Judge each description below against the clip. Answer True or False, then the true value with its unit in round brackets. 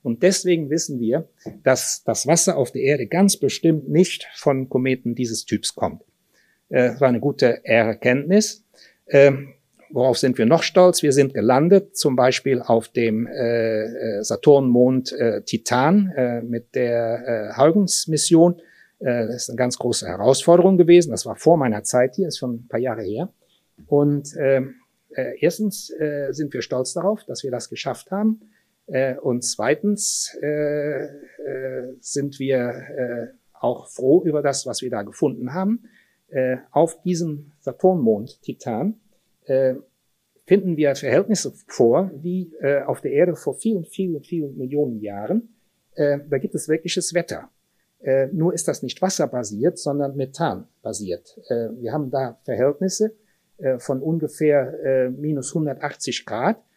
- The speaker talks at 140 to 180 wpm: True (150 wpm)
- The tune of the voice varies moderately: False (5.7 semitones)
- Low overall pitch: False (145 Hz)